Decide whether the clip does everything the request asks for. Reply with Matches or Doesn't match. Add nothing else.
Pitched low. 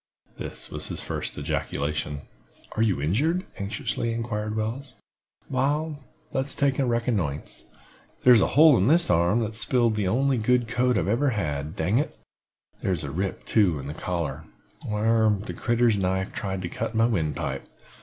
Matches